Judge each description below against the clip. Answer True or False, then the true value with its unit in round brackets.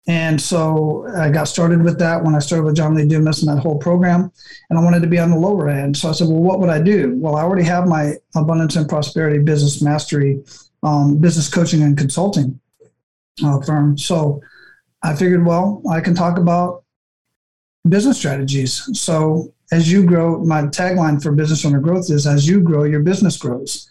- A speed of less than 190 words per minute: False (200 wpm)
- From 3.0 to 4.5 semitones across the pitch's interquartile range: False (2.6 semitones)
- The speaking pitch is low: False (160 Hz)